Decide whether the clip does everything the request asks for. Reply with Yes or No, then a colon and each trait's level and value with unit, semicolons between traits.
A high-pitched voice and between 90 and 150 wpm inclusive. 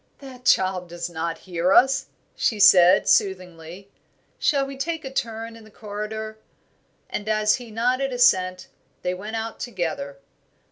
Yes: high, 210 Hz; average, 145 wpm